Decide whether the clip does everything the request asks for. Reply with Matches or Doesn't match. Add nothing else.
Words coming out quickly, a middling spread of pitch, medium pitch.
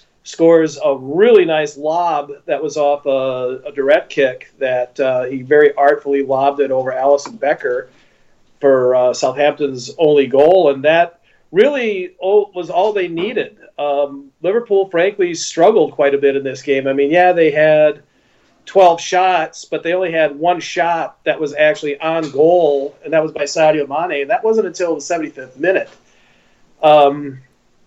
Doesn't match